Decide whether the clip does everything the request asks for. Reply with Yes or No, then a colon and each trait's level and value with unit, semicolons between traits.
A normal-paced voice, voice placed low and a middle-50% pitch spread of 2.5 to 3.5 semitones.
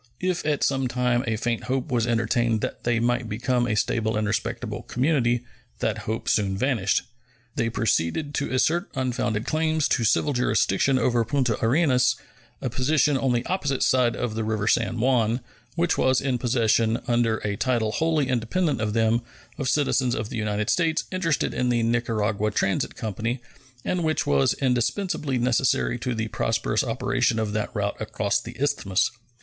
Yes: average, 170 wpm; low, 120 Hz; average, 3.2 semitones